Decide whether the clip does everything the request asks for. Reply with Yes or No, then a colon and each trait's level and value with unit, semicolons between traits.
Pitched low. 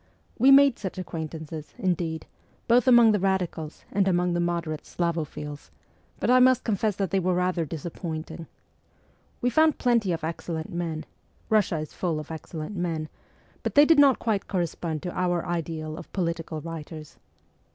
No: medium, 175 Hz